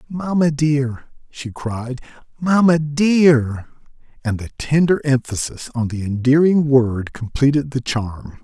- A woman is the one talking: No, male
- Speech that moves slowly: Yes, slow, 120 wpm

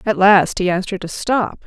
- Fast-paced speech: Yes, fast, 250 wpm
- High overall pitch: Yes, high, 195 Hz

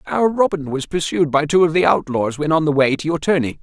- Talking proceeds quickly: Yes, fast, 265 wpm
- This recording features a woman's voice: No, male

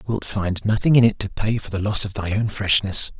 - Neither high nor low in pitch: No, low, 105 Hz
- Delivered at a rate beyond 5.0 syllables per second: Yes, 5.3 syllables/s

